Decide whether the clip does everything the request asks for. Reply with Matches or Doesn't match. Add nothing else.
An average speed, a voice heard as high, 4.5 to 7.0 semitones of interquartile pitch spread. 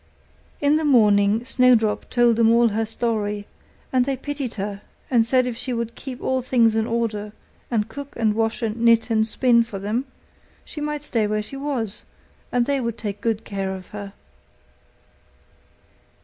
Doesn't match